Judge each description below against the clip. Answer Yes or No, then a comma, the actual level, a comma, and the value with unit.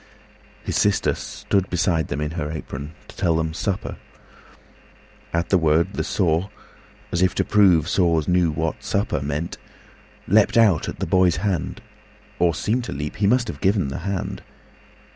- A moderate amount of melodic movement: Yes, average, 3.7 semitones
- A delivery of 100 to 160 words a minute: Yes, average, 150 wpm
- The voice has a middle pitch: No, very low, 85 Hz